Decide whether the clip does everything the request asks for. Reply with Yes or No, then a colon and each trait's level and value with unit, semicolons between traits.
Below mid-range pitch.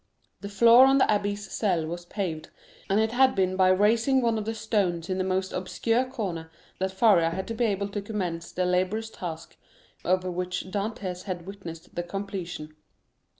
No: high, 190 Hz